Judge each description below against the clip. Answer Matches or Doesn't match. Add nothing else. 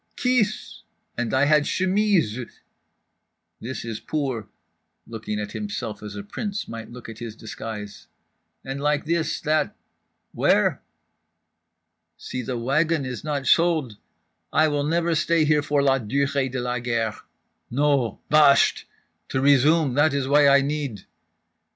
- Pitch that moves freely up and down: Doesn't match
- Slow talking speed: Matches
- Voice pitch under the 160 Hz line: Matches